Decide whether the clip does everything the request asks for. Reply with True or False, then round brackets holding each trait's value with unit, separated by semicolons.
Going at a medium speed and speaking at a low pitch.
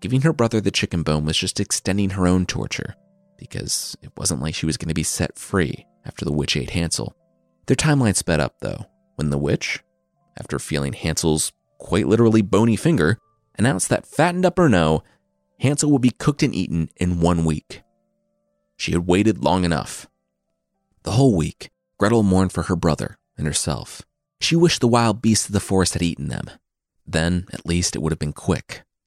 True (190 wpm; 95 Hz)